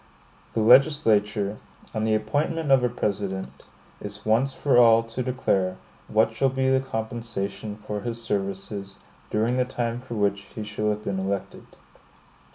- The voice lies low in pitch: Yes, low, 110 Hz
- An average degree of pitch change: Yes, average, 3.3 semitones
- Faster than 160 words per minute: No, average, 155 wpm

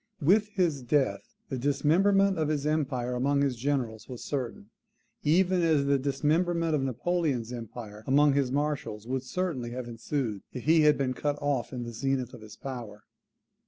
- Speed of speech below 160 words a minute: No, average, 170 wpm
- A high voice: No, medium, 140 Hz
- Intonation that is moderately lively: Yes, average, 3.8 semitones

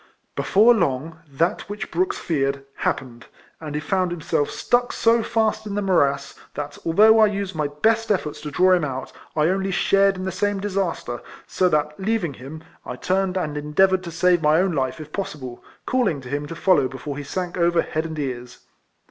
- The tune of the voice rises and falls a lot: No, average, 5.0 semitones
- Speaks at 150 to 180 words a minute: No, average, 200 wpm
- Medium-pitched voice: Yes, medium, 170 Hz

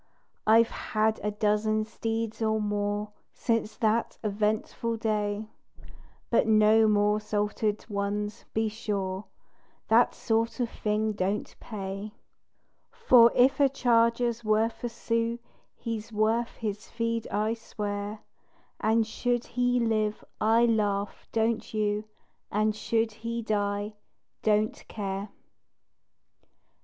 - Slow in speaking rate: Yes, slow, 115 wpm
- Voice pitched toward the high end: Yes, high, 215 Hz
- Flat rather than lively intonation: Yes, narrow, 1.6 semitones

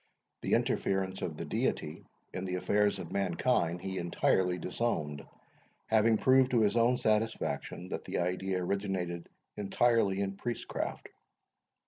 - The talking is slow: Yes, slow, 130 wpm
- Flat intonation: No, average, 3.6 semitones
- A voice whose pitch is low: Yes, very low, 95 Hz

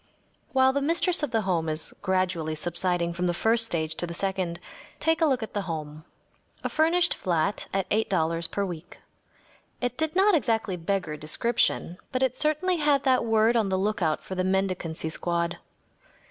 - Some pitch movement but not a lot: No, wide, 7.0 semitones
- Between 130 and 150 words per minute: No, average, 175 wpm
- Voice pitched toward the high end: Yes, high, 195 Hz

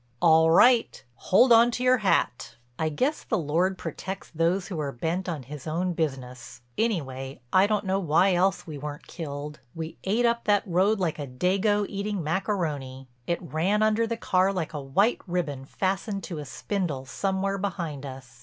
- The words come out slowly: No, average, 175 wpm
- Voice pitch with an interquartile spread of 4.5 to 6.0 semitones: Yes, average, 5.1 semitones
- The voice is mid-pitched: Yes, medium, 175 Hz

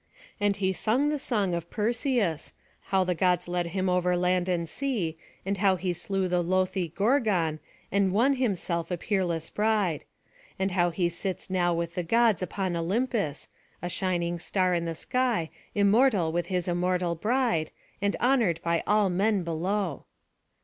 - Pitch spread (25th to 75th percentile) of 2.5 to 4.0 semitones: Yes, average, 3.3 semitones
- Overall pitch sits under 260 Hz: Yes, medium, 185 Hz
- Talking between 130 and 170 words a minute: Yes, average, 165 wpm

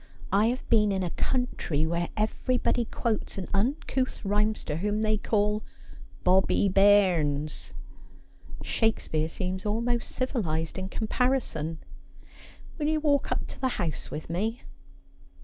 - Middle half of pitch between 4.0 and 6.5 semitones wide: Yes, average, 5.1 semitones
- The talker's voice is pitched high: Yes, high, 210 Hz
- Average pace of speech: No, slow, 125 wpm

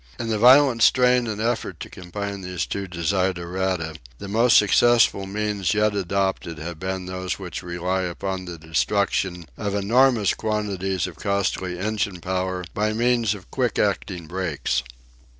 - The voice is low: Yes, very low, 95 Hz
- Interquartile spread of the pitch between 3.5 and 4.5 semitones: No, average, 2.8 semitones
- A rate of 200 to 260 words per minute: No, average, 150 wpm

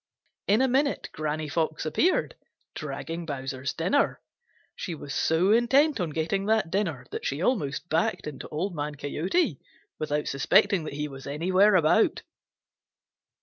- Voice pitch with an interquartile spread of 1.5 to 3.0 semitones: No, average, 5.1 semitones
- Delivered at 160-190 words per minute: No, average, 145 wpm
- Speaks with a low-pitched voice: No, medium, 160 Hz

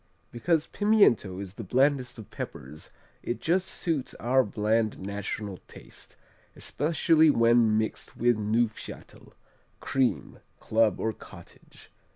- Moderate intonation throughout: Yes, average, 4.9 semitones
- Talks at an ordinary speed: No, slow, 120 wpm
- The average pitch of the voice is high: No, low, 115 Hz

